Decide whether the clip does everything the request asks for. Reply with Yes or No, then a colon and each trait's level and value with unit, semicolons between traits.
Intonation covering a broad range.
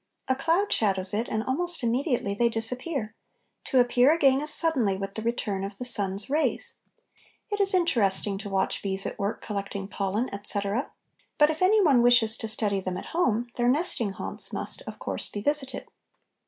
Yes: wide, 6.1 semitones